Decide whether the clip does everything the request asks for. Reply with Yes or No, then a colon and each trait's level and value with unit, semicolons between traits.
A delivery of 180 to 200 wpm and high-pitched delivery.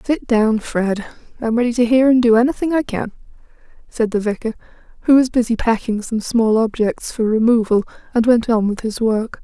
Yes: average, 190 wpm; high, 230 Hz